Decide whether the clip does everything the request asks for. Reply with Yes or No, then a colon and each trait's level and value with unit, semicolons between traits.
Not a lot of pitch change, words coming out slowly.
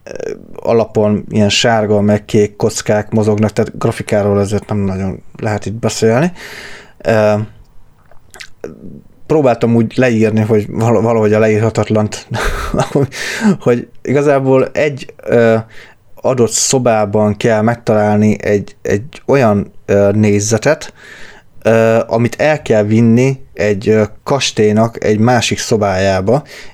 Yes: narrow, 1.9 semitones; slow, 95 wpm